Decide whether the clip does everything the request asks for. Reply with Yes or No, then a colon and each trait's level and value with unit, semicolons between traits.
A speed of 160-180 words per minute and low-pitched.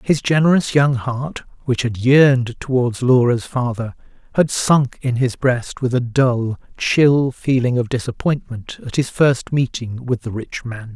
Yes: average, 165 wpm; low, 125 Hz